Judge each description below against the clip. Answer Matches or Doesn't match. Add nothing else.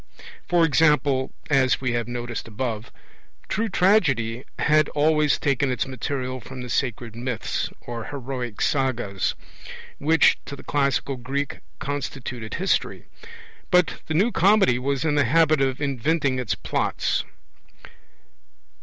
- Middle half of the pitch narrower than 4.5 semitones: Matches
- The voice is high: Doesn't match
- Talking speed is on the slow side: Matches